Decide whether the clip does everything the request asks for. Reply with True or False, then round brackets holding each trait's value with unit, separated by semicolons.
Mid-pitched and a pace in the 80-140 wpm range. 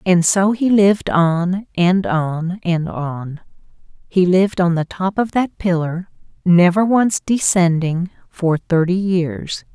True (180 Hz; 135 wpm)